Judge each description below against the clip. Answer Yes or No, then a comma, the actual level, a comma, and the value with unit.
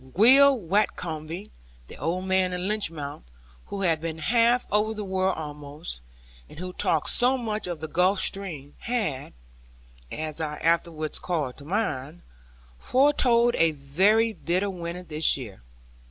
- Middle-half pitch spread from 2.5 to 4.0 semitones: No, average, 5.2 semitones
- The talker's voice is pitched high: No, medium, 180 Hz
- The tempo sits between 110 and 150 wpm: Yes, average, 140 wpm